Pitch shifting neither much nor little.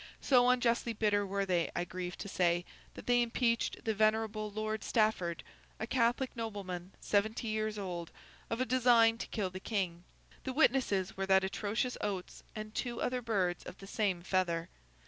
Yes: average, 3.7 semitones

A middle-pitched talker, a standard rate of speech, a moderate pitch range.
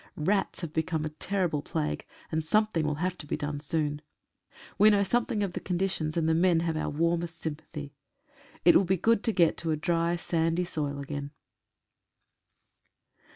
Yes: medium, 165 Hz; average, 175 wpm; average, 3.0 semitones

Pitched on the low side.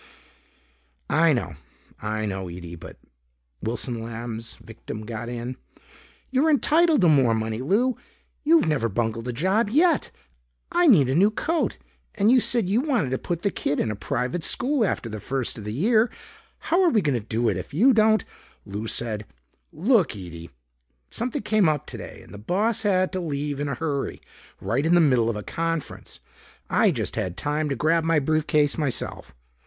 No: medium, 145 Hz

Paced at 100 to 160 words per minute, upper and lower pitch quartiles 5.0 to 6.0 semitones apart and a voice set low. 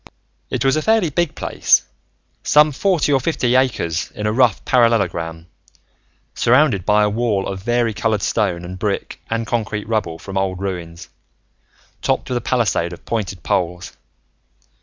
Yes: average, 150 wpm; average, 5.3 semitones; low, 110 Hz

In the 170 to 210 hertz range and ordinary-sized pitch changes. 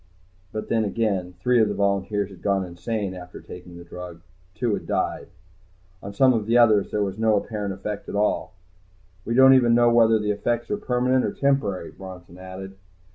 No: low, 105 Hz; average, 3.6 semitones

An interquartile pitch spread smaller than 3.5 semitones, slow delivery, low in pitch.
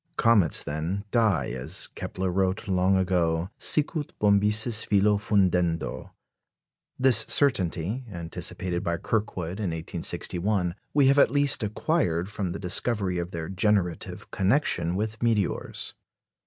No: average, 3.8 semitones; slow, 120 wpm; very low, 95 Hz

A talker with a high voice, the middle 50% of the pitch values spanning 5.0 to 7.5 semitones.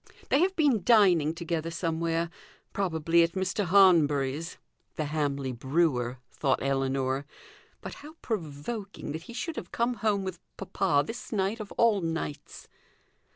No: medium, 170 Hz; wide, 5.5 semitones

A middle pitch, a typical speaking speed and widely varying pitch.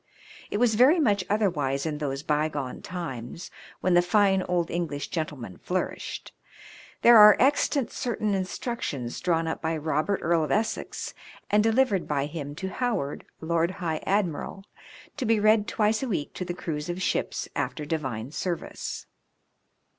Yes: medium, 175 Hz; average, 160 wpm; wide, 5.8 semitones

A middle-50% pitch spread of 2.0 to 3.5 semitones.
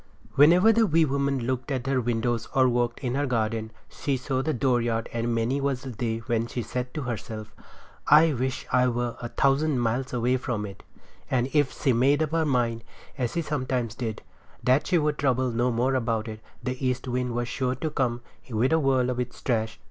Yes: narrow, 2.5 semitones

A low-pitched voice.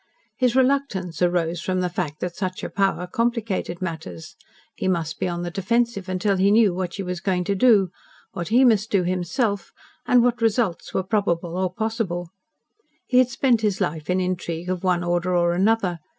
No: medium, 185 Hz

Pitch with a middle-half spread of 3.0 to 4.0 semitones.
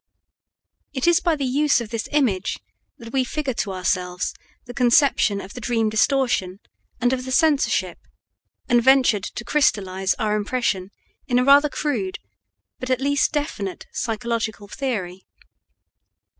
No: average, 5.0 semitones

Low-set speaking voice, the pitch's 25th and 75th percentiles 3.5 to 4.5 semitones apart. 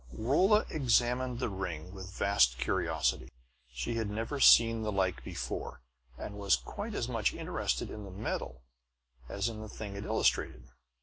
Yes: low, 100 Hz; average, 3.8 semitones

